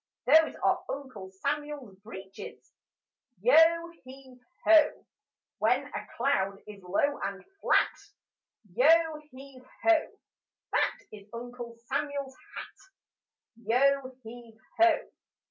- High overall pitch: Yes, very high, 260 Hz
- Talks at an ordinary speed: No, slow, 100 wpm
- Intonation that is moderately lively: Yes, average, 4.9 semitones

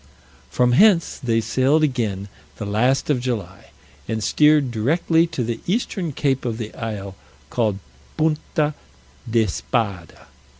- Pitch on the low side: Yes, low, 125 Hz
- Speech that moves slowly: Yes, slow, 125 wpm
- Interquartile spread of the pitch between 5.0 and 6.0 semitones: Yes, wide, 5.5 semitones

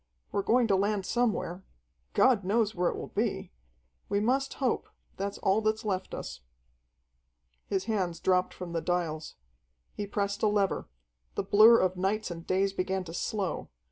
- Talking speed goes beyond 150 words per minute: Yes, average, 165 wpm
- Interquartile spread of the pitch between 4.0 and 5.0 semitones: No, average, 2.7 semitones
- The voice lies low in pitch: No, high, 195 Hz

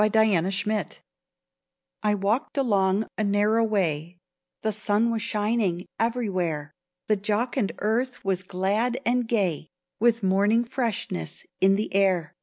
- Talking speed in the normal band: No, slow, 130 wpm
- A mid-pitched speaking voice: No, high, 210 Hz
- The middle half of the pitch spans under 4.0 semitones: Yes, average, 3.0 semitones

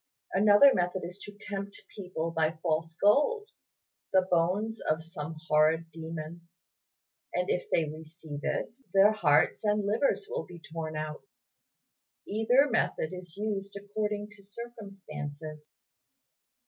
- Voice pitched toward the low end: No, medium, 185 Hz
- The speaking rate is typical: No, slow, 125 wpm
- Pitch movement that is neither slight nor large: Yes, average, 4.5 semitones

